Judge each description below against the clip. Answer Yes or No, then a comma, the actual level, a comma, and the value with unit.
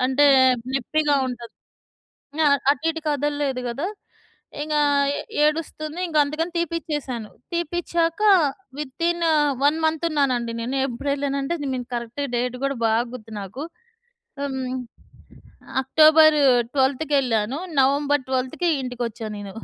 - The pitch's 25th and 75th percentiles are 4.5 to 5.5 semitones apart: No, average, 3.6 semitones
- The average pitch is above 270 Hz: Yes, very high, 280 Hz